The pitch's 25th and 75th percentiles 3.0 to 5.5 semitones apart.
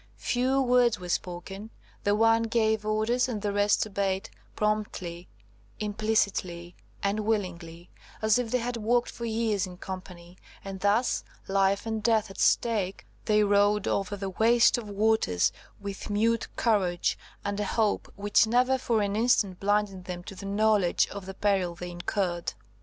No: narrow, 2.6 semitones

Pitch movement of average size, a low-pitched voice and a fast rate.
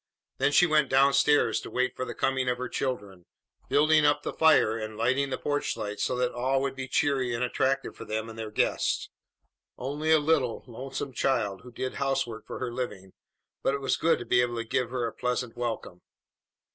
Yes: average, 3.0 semitones; low, 130 Hz; fast, 210 wpm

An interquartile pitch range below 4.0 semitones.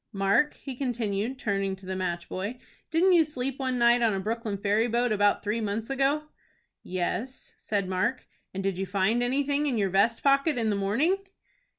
No: average, 5.0 semitones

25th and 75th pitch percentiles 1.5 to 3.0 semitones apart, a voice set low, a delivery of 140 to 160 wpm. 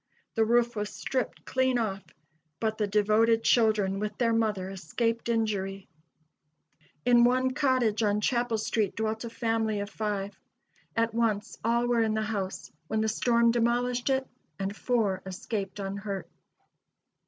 No: narrow, 2.4 semitones; high, 220 Hz; average, 145 wpm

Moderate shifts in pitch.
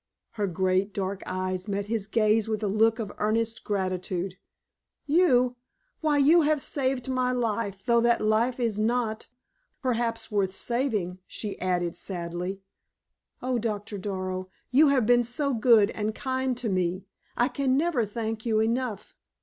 Yes: average, 4.0 semitones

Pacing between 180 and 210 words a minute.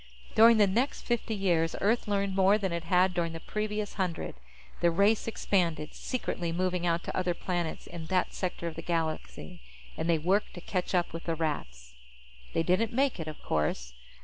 Yes: average, 190 wpm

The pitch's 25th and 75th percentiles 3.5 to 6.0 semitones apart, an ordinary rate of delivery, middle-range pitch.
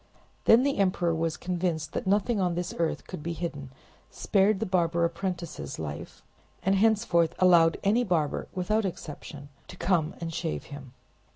No: average, 3.1 semitones; average, 160 wpm; medium, 175 Hz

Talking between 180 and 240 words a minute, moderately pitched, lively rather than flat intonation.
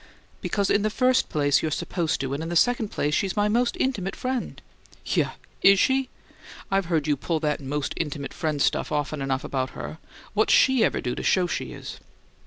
Yes: average, 200 wpm; medium, 170 Hz; wide, 6.3 semitones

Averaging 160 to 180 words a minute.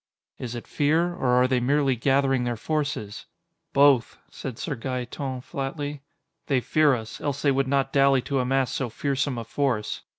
Yes: average, 170 wpm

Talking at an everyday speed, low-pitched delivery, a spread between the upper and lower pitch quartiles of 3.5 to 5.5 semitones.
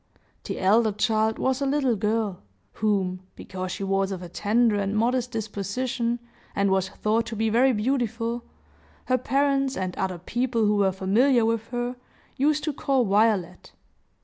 No: average, 160 wpm; high, 225 Hz; average, 3.8 semitones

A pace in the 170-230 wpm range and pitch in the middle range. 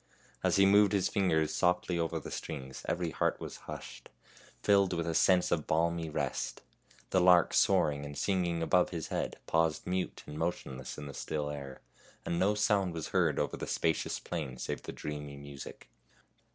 No: average, 180 wpm; very low, 85 Hz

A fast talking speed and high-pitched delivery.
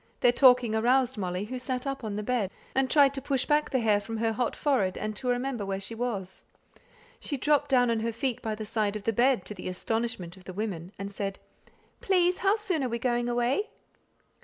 Yes: fast, 225 wpm; high, 235 Hz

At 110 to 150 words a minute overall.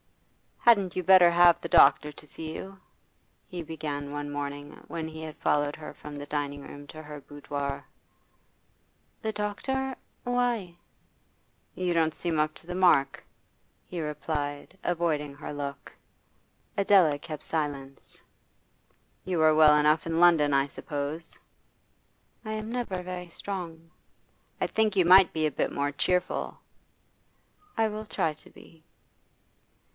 Yes: average, 140 wpm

